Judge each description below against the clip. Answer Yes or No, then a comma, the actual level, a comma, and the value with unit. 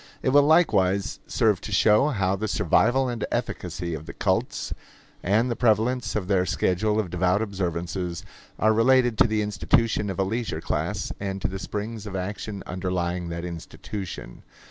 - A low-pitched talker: Yes, low, 100 Hz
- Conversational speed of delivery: Yes, average, 165 wpm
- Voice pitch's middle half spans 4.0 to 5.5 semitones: No, average, 3.6 semitones